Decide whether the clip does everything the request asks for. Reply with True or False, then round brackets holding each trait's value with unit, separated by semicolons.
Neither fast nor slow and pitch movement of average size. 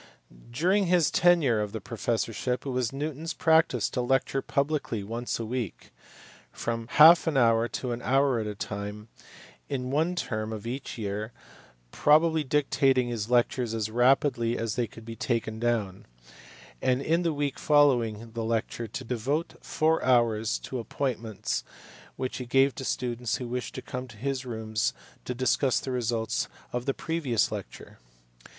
True (165 wpm; 3.5 semitones)